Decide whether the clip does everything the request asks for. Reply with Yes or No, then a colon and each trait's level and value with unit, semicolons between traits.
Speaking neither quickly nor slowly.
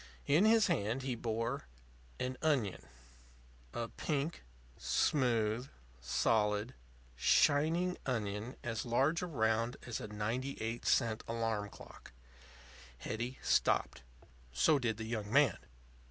No: slow, 110 wpm